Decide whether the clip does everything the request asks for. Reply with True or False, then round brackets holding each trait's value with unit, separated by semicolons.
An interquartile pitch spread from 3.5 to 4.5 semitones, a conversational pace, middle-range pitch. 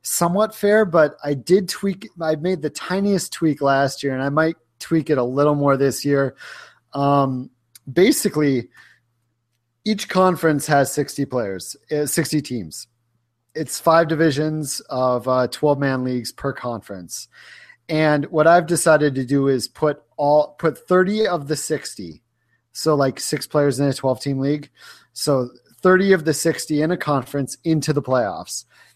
True (3.8 semitones; 160 wpm; 145 Hz)